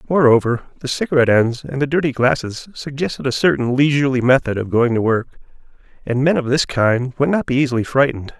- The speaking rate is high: No, average, 195 wpm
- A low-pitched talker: Yes, low, 130 Hz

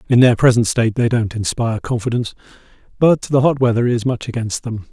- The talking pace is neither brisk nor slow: Yes, average, 195 wpm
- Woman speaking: No, male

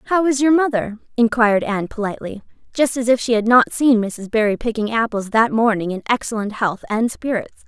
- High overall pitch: Yes, high, 230 Hz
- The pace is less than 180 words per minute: No, average, 195 wpm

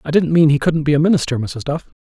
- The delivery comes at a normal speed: No, fast, 295 wpm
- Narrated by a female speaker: No, male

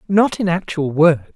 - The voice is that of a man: Yes, male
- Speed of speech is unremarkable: Yes, average, 175 wpm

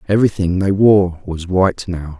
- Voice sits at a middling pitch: No, very low, 95 Hz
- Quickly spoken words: No, average, 165 wpm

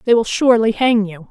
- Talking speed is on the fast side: Yes, fast, 230 wpm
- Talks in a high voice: Yes, high, 220 Hz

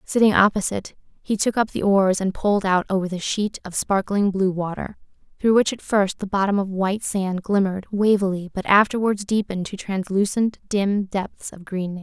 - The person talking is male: No, female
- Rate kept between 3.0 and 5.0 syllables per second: No, 5.3 syllables/s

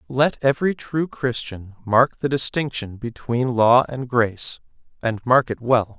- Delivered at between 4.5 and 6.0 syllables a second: No, 4.2 syllables/s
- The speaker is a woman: No, male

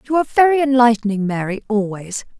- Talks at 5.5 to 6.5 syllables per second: Yes, 6.3 syllables/s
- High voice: Yes, high, 235 Hz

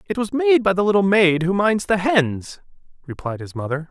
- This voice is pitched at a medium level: Yes, medium, 170 Hz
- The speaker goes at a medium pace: No, fast, 215 wpm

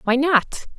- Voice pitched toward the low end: No, very high, 270 Hz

